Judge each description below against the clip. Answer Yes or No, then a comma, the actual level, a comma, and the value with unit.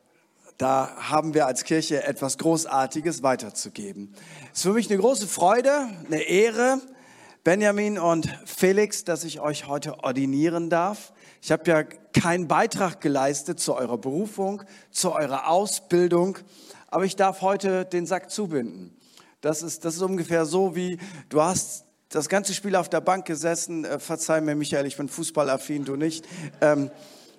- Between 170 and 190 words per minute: No, average, 155 wpm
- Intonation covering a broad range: No, average, 4.0 semitones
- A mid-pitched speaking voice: Yes, medium, 165 Hz